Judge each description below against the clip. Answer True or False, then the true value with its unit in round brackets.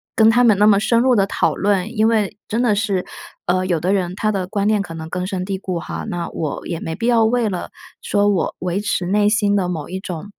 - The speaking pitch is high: True (200 Hz)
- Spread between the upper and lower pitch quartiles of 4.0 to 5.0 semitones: False (3.0 semitones)